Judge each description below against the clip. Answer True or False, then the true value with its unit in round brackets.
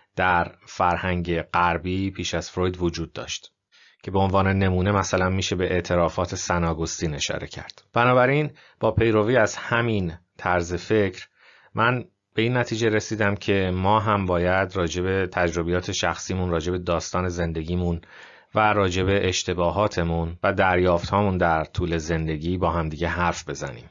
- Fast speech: False (135 wpm)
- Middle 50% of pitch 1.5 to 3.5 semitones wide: True (2.5 semitones)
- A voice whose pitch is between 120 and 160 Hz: False (90 Hz)